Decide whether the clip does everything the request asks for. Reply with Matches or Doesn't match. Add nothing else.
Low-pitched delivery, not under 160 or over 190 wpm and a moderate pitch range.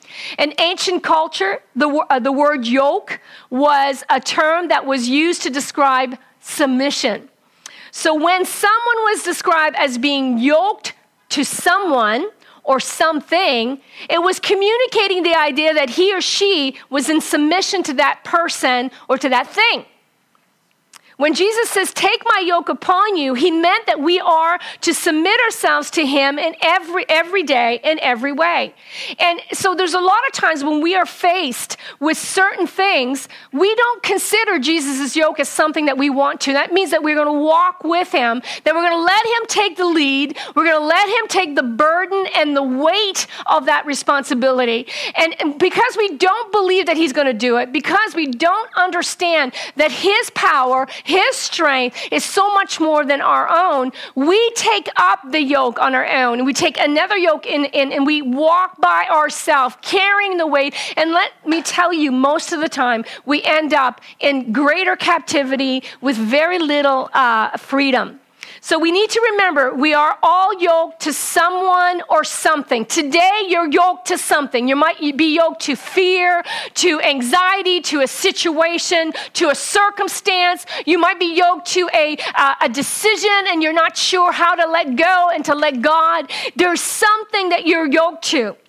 Doesn't match